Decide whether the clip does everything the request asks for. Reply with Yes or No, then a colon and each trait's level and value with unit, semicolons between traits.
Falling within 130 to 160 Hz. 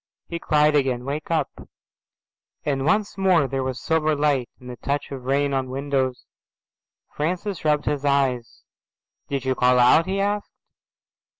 Yes: medium, 140 Hz